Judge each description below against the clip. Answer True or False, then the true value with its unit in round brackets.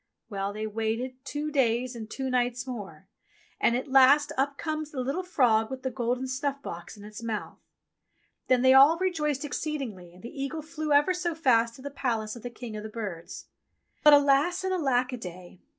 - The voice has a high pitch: True (255 Hz)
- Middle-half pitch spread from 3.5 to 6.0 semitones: True (4.4 semitones)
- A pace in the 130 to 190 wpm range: False (200 wpm)